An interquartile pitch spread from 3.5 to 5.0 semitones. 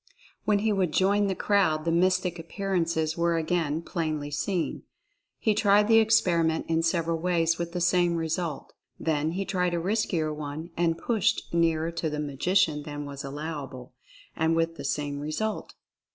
No: average, 2.9 semitones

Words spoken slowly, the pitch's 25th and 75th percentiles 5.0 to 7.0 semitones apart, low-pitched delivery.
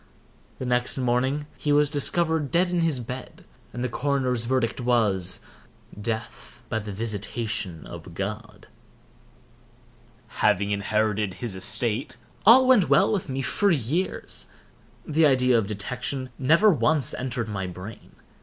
Yes: slow, 130 wpm; wide, 5.4 semitones; low, 125 Hz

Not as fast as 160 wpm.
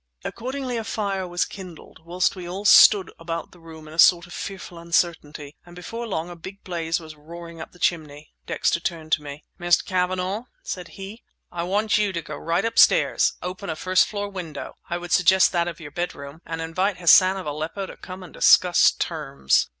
No: average, 195 wpm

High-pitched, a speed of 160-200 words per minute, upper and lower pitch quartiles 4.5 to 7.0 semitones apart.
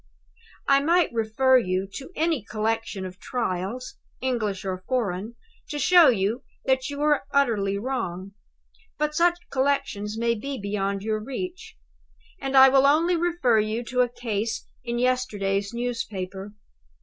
No: high, 235 Hz; slow, 135 wpm; average, 5.1 semitones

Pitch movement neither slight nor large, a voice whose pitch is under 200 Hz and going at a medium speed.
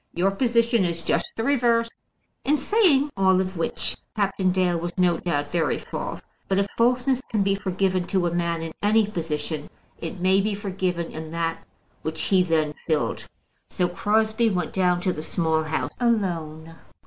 Yes: average, 4.2 semitones; medium, 185 Hz; average, 170 wpm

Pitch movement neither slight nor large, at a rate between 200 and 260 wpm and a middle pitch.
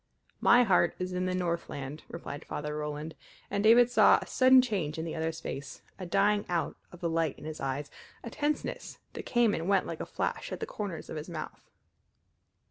Yes: average, 4.9 semitones; fast, 205 wpm; medium, 170 Hz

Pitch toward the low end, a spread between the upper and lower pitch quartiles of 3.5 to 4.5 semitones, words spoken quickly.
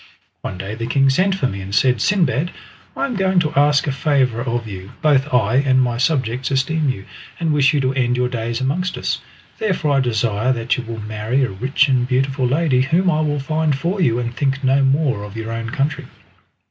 Yes: low, 130 Hz; average, 3.9 semitones; fast, 220 wpm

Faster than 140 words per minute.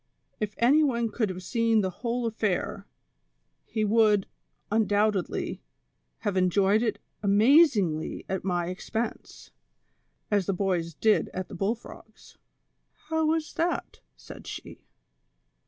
No: slow, 135 wpm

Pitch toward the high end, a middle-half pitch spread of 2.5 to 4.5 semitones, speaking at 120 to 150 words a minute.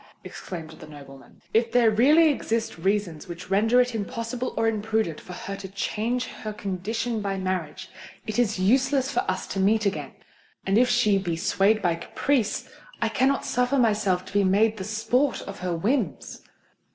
No: high, 210 Hz; average, 3.9 semitones; average, 170 wpm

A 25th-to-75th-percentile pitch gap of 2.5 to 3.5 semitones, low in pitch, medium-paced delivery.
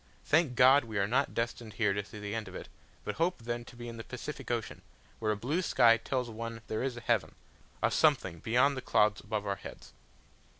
No: average, 2.9 semitones; low, 115 Hz; fast, 225 wpm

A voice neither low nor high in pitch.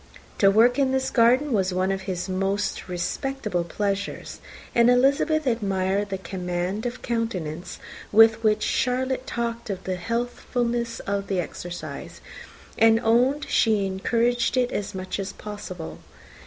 No: high, 215 Hz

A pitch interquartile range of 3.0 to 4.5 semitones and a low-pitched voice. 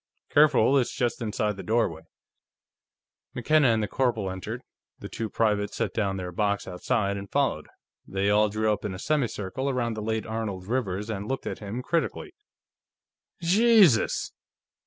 Yes: average, 4.1 semitones; low, 110 Hz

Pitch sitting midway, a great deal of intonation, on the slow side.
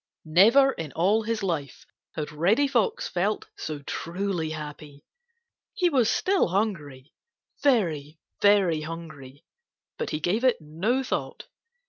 Yes: medium, 175 Hz; wide, 6.7 semitones; slow, 120 wpm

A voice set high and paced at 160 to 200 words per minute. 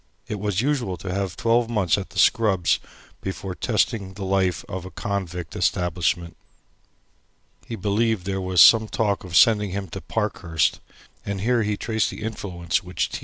No: very low, 95 Hz; average, 170 wpm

